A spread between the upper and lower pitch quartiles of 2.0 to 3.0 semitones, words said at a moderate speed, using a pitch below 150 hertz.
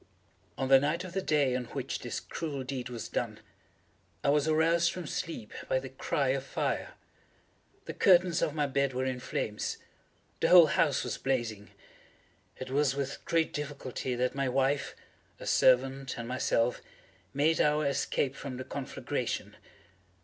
Yes: narrow, 2.6 semitones; average, 160 wpm; low, 135 Hz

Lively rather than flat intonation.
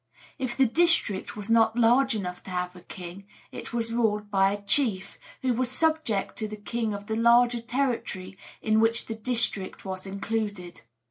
No: average, 3.3 semitones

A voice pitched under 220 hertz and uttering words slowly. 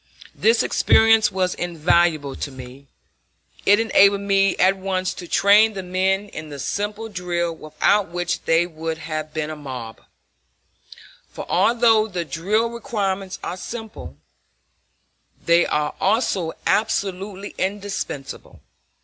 Yes: medium, 185 Hz; slow, 125 wpm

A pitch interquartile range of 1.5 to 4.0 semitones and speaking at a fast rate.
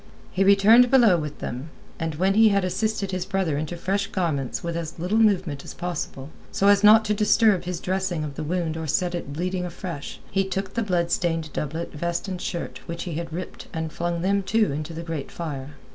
Yes: average, 3.3 semitones; fast, 215 wpm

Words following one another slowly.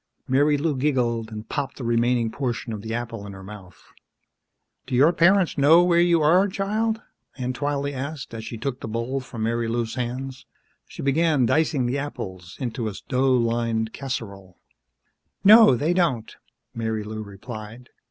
No: average, 155 wpm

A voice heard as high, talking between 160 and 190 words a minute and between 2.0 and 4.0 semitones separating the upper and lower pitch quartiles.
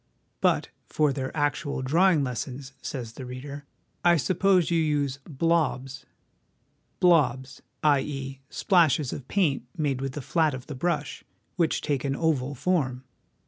No: medium, 140 Hz; average, 165 wpm; average, 3.6 semitones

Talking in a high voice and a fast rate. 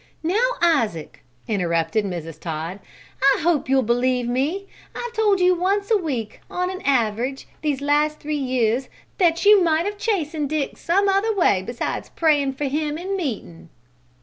No: very high, 295 Hz; average, 160 wpm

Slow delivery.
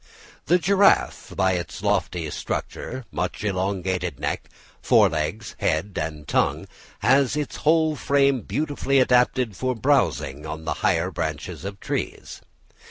Yes: slow, 130 wpm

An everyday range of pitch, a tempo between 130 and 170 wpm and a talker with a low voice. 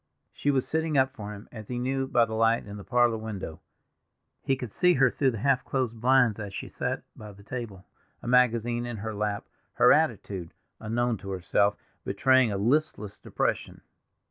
No: average, 3.8 semitones; average, 190 wpm; low, 115 Hz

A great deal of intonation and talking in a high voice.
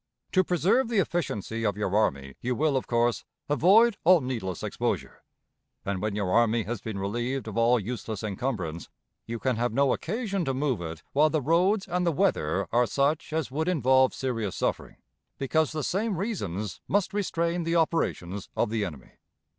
No: wide, 7.8 semitones; low, 130 Hz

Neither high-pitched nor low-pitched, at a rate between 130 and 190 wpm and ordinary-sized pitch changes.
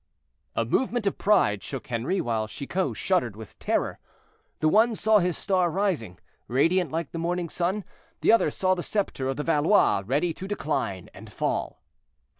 No: medium, 170 Hz; average, 170 wpm; wide, 6.5 semitones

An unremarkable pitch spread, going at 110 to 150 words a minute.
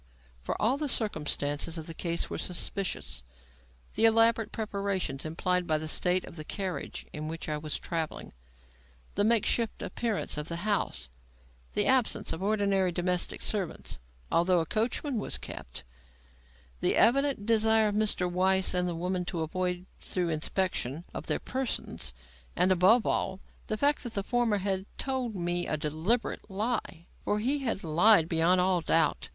No: average, 4.6 semitones; average, 160 wpm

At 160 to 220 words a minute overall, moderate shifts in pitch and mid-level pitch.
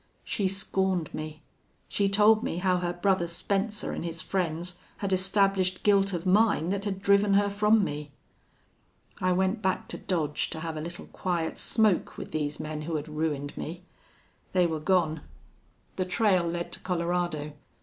Yes: average, 170 wpm; average, 3.3 semitones; medium, 180 Hz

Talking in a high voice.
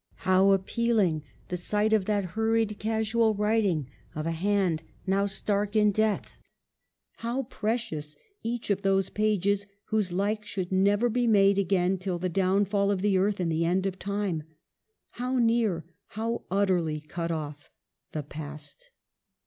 Yes: high, 200 Hz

